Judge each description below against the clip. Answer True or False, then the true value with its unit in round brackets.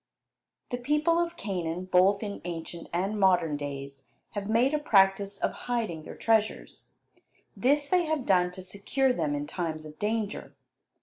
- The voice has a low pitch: False (200 Hz)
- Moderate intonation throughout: False (6.1 semitones)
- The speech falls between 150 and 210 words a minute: True (160 wpm)